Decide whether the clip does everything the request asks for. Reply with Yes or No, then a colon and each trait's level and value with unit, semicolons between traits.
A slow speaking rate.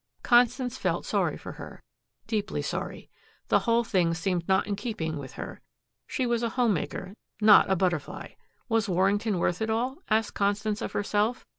No: average, 170 wpm